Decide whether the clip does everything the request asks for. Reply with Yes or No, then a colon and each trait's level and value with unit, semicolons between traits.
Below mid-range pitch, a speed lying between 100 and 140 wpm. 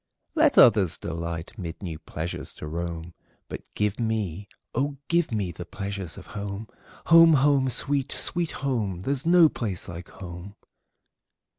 Yes: low, 100 Hz; slow, 135 wpm